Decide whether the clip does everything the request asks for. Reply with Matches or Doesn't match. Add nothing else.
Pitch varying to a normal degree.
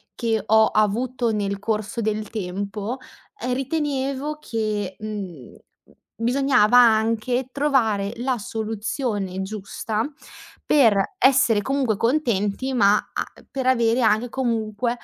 Matches